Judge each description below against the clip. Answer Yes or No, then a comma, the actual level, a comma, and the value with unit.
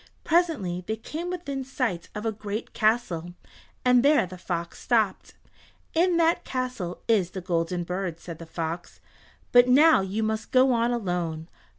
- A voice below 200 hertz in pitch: No, high, 215 Hz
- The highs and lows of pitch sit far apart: Yes, wide, 6.3 semitones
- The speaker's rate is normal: Yes, average, 160 wpm